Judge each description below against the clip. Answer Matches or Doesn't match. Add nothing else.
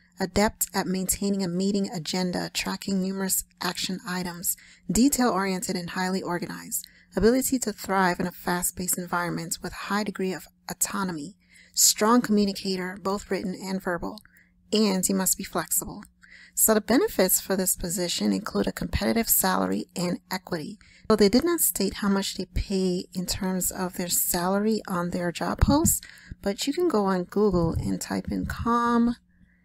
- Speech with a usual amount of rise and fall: Doesn't match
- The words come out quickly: Doesn't match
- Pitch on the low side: Doesn't match